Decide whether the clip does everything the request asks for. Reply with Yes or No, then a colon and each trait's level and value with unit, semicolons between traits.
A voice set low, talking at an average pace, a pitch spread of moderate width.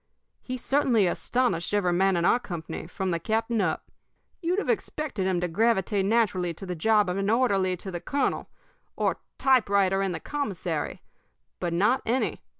No: high, 195 Hz; average, 170 wpm; average, 4.7 semitones